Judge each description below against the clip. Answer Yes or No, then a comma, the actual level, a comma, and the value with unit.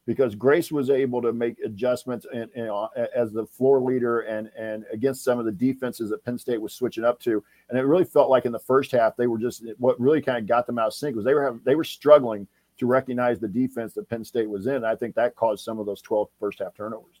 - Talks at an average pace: No, fast, 270 wpm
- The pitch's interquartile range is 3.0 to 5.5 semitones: No, narrow, 2.6 semitones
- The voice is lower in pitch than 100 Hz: No, low, 120 Hz